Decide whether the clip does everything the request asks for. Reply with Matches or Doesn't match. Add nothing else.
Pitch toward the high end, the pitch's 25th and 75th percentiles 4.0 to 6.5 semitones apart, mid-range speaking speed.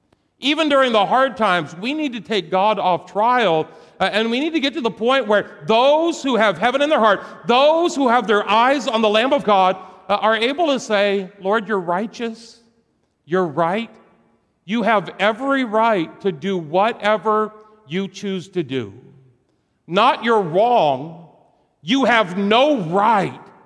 Matches